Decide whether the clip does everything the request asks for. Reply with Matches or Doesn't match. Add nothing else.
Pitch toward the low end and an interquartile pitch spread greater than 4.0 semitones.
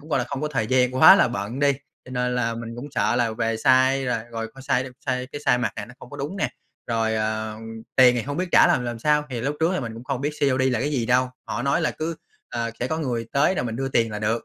Doesn't match